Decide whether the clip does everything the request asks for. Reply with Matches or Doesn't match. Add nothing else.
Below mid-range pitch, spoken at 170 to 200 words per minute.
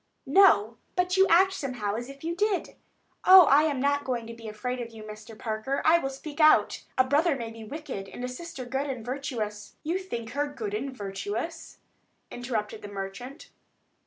Doesn't match